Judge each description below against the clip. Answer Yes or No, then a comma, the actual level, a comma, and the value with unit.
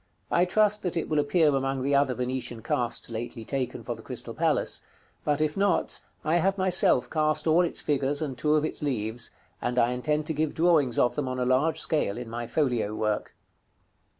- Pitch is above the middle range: No, medium, 140 Hz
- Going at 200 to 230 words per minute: Yes, fast, 205 wpm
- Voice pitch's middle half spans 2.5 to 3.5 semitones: No, average, 4.2 semitones